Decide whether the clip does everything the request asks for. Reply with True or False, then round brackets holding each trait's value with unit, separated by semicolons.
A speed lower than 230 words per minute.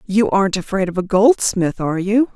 True (205 wpm)